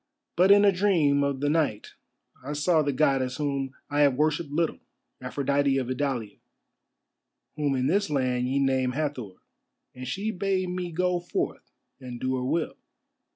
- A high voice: No, medium, 145 Hz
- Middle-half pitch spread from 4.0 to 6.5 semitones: Yes, average, 4.3 semitones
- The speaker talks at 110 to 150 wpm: No, average, 160 wpm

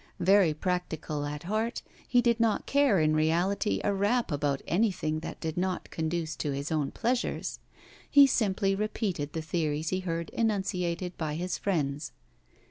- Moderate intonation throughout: Yes, average, 4.7 semitones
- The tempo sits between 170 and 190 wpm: No, average, 155 wpm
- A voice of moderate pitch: Yes, medium, 175 Hz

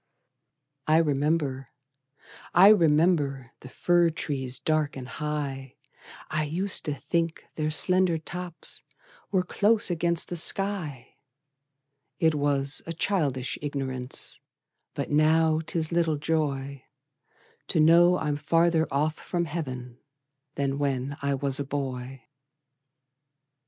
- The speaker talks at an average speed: No, slow, 115 wpm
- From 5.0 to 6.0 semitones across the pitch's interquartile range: No, average, 3.5 semitones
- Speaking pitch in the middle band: Yes, medium, 150 Hz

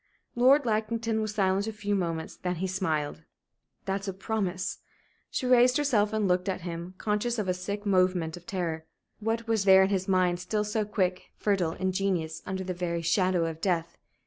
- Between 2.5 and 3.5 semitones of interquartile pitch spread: Yes, average, 2.9 semitones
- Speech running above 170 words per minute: Yes, average, 185 wpm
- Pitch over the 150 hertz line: Yes, high, 190 Hz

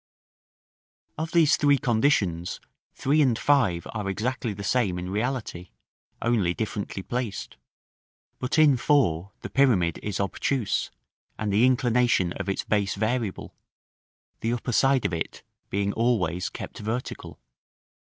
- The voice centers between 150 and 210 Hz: No, low, 110 Hz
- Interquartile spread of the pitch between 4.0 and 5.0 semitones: Yes, average, 4.7 semitones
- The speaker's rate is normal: No, slow, 130 wpm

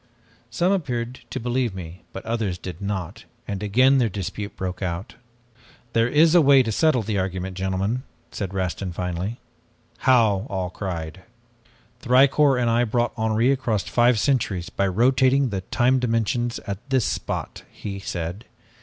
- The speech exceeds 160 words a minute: No, average, 155 wpm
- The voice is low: Yes, low, 110 Hz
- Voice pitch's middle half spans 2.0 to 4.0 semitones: No, average, 4.9 semitones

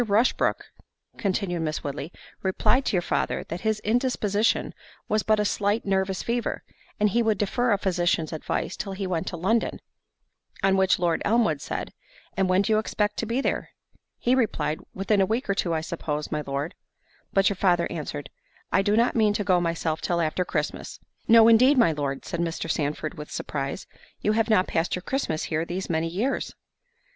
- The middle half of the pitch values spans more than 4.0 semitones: Yes, average, 4.6 semitones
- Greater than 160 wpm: Yes, average, 185 wpm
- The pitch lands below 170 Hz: No, high, 190 Hz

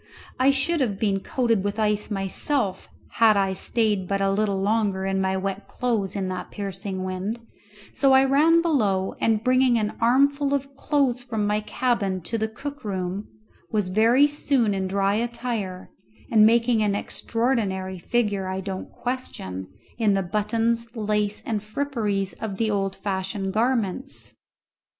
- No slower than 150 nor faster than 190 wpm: Yes, average, 155 wpm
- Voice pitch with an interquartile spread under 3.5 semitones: No, average, 3.8 semitones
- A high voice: Yes, high, 215 Hz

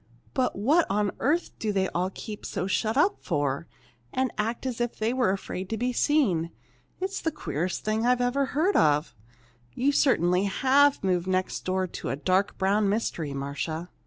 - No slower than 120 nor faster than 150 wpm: No, average, 180 wpm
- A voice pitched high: Yes, high, 210 Hz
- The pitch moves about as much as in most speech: No, wide, 6.1 semitones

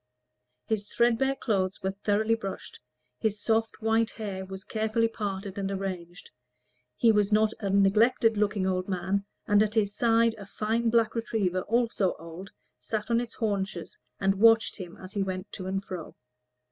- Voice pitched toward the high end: Yes, high, 205 Hz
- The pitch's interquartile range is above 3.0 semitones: No, average, 2.7 semitones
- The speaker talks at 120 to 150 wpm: No, average, 165 wpm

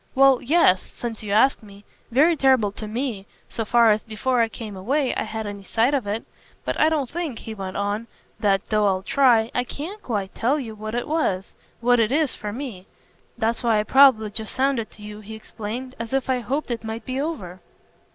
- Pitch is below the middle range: No, high, 230 Hz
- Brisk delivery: Yes, fast, 215 wpm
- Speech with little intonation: No, average, 3.9 semitones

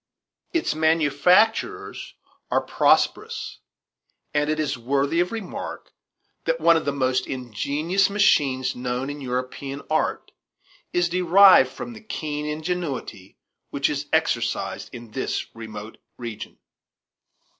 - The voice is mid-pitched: Yes, medium, 145 Hz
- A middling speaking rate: No, slow, 115 wpm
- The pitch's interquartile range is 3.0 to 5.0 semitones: No, wide, 5.6 semitones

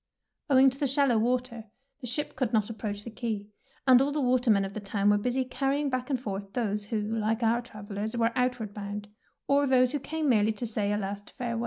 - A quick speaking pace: Yes, fast, 220 wpm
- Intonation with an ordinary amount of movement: Yes, average, 3.6 semitones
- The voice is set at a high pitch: Yes, high, 235 Hz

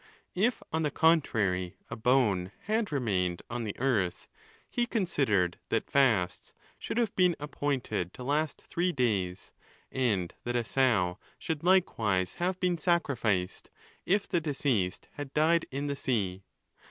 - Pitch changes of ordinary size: No, wide, 8.9 semitones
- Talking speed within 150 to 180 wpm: No, average, 140 wpm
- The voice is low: Yes, low, 130 Hz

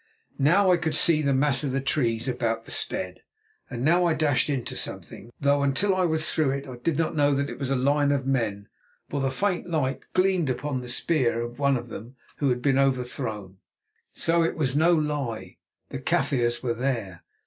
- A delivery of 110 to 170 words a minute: No, fast, 205 wpm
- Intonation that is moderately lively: Yes, average, 3.9 semitones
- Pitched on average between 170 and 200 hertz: No, low, 135 Hz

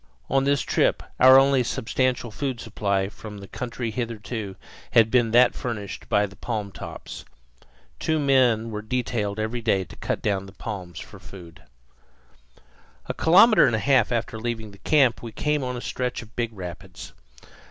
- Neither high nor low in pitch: No, low, 115 Hz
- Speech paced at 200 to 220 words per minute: No, average, 165 wpm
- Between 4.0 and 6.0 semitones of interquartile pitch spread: No, average, 3.6 semitones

